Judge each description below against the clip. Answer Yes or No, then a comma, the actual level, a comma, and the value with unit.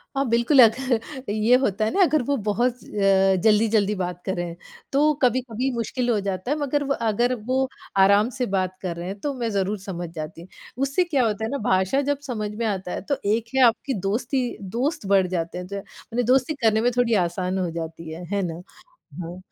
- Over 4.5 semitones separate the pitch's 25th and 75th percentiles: Yes, average, 5.2 semitones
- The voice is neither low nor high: No, high, 215 Hz